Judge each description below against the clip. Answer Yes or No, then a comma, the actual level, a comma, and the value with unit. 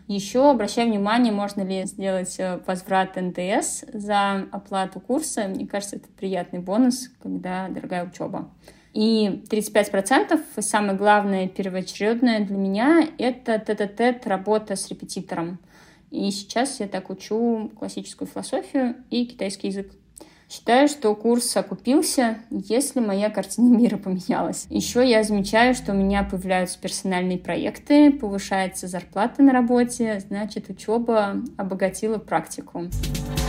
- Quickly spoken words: No, average, 120 wpm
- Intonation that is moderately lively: Yes, average, 3.8 semitones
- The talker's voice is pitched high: Yes, high, 205 Hz